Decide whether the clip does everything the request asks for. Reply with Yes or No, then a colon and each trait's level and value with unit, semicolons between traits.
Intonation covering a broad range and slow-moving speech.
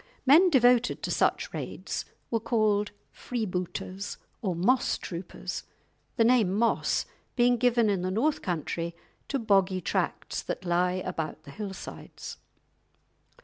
No: average, 4.7 semitones; slow, 125 wpm